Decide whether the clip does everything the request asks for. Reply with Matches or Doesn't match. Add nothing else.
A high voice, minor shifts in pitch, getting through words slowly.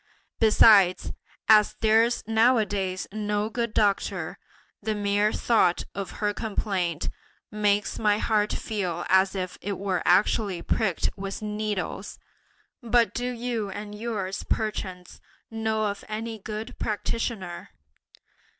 Matches